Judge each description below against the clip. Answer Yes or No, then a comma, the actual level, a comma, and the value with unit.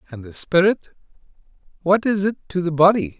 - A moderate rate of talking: Yes, average, 150 wpm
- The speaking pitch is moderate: Yes, medium, 175 Hz